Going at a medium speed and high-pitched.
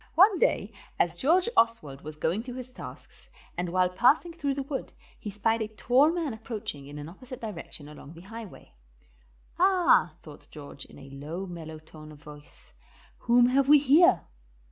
Yes: average, 175 wpm; high, 210 Hz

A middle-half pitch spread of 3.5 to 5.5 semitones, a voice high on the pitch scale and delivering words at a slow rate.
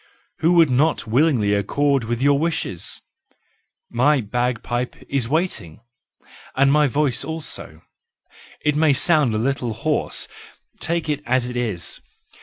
No: average, 4.1 semitones; low, 135 Hz; slow, 125 wpm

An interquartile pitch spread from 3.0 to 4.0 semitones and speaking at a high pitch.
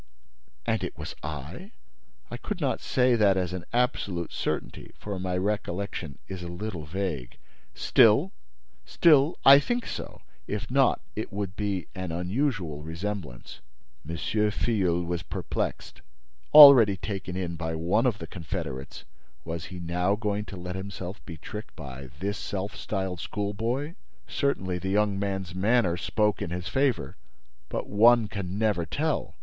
No: average, 3.7 semitones; very low, 95 Hz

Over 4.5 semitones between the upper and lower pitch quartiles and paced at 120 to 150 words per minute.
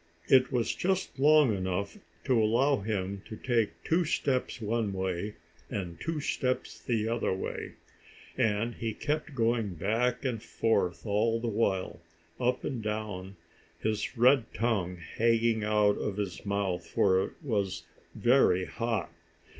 No: average, 3.5 semitones; average, 140 wpm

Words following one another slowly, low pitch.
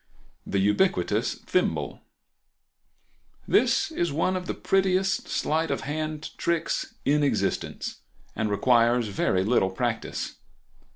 No: slow, 105 wpm; medium, 145 Hz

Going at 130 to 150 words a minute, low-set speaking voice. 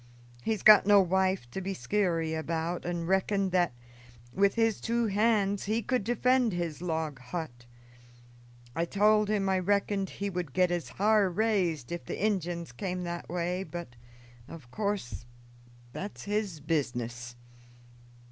No: average, 145 wpm; medium, 185 Hz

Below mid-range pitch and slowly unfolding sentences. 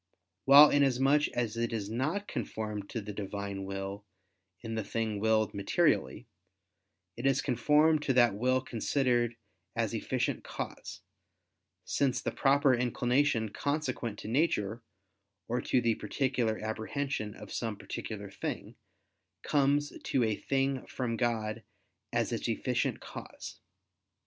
Yes: low, 120 Hz; slow, 130 wpm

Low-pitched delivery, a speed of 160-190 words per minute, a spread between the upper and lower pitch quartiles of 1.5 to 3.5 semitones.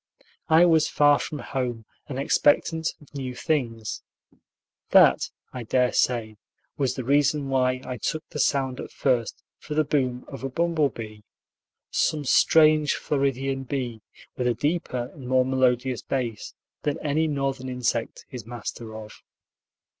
No: low, 130 Hz; average, 145 wpm; average, 2.9 semitones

